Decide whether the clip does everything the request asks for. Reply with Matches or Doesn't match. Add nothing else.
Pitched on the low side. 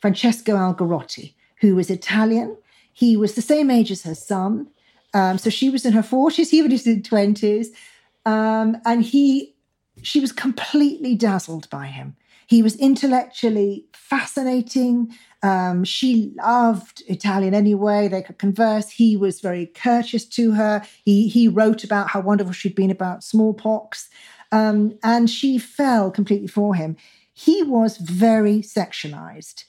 Doesn't match